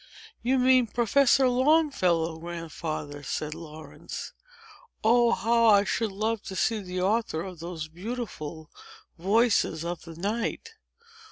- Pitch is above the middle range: Yes, high, 200 Hz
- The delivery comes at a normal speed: No, slow, 120 wpm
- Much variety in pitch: Yes, wide, 6.1 semitones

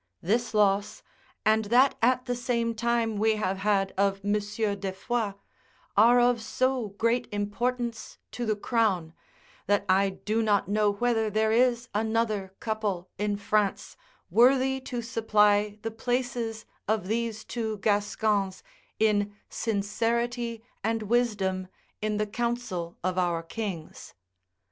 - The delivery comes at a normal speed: No, slow, 130 wpm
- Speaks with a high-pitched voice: Yes, high, 215 Hz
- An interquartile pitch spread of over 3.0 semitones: No, narrow, 2.5 semitones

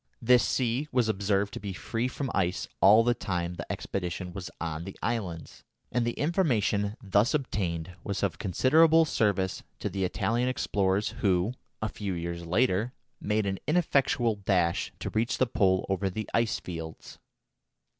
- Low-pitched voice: Yes, low, 100 Hz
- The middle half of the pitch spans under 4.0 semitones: No, average, 4.4 semitones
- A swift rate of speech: No, average, 160 wpm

